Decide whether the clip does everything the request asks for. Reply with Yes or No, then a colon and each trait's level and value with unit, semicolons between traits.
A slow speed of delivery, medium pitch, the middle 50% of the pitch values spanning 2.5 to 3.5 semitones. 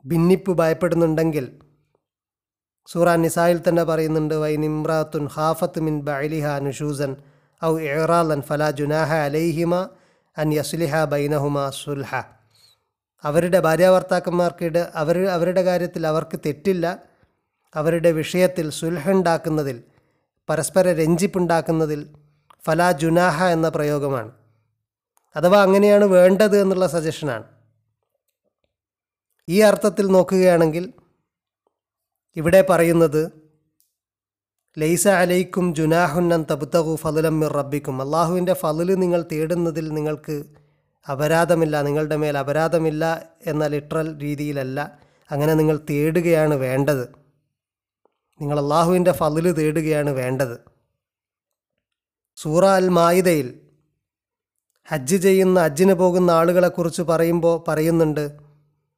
No: average, 90 wpm; medium, 160 Hz; average, 2.8 semitones